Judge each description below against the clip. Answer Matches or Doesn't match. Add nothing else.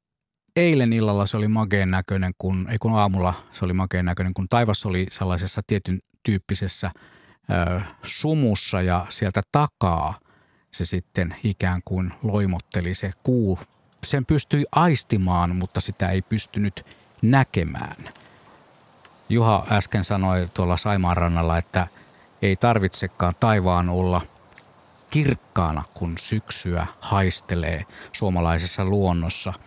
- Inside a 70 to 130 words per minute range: Matches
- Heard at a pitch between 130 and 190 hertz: Doesn't match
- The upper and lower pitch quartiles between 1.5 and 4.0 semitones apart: Matches